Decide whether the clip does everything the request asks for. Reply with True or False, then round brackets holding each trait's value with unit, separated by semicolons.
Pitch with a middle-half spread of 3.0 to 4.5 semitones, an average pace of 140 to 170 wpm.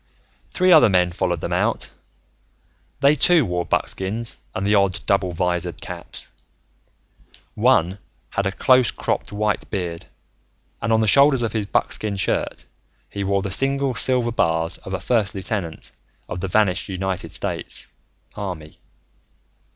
True (4.2 semitones; 145 wpm)